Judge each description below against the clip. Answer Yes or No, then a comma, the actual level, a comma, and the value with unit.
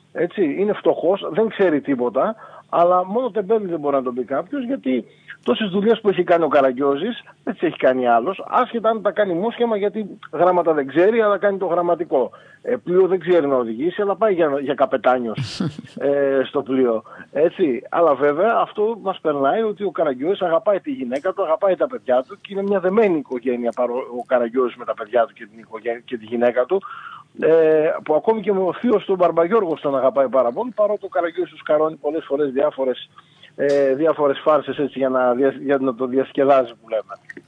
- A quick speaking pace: Yes, fast, 200 wpm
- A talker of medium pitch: Yes, medium, 160 Hz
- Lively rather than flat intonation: Yes, wide, 7.2 semitones